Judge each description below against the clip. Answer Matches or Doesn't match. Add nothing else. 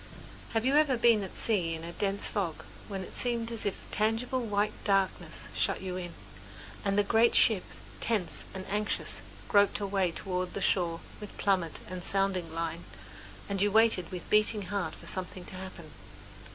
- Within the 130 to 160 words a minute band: Doesn't match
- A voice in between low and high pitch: Doesn't match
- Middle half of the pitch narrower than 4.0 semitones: Matches